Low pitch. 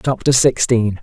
Yes: low, 120 Hz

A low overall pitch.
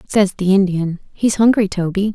No: high, 195 Hz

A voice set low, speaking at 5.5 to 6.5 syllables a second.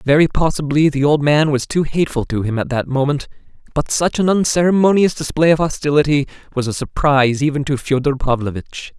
No: medium, 145 Hz; 5.8 syllables/s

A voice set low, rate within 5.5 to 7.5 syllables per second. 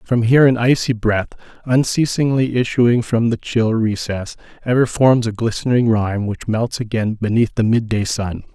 No: low, 115 Hz; 4.7 syllables/s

